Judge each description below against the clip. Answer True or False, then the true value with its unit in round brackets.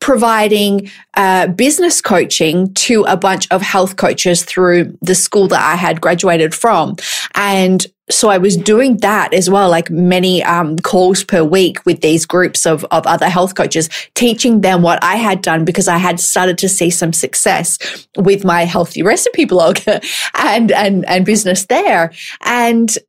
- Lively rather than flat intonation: False (2.8 semitones)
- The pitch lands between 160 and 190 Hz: True (185 Hz)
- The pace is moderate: True (170 wpm)